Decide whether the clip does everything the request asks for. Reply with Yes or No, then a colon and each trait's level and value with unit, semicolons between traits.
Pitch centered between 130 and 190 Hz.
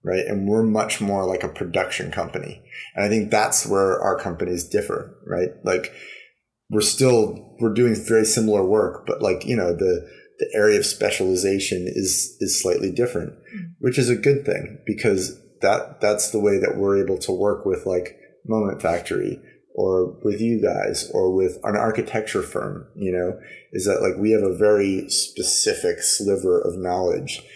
No: low, 110 Hz